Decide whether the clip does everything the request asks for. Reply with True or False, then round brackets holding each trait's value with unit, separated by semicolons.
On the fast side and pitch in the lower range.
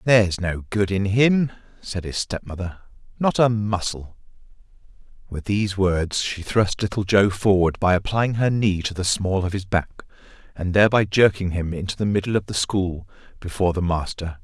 False (175 wpm; 95 Hz)